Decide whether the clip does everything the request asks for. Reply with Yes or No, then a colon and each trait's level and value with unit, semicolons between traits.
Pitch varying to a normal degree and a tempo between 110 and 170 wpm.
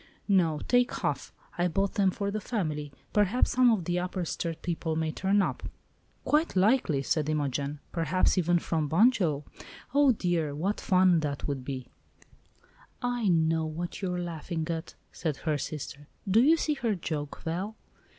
Yes: average, 4.4 semitones; average, 165 wpm